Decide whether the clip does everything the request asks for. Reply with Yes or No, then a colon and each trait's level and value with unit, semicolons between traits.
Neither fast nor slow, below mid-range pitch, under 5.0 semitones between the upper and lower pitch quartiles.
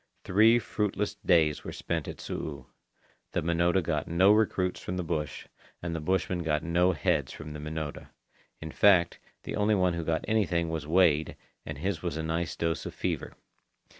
Yes: average, 180 wpm; very low, 85 Hz; average, 2.8 semitones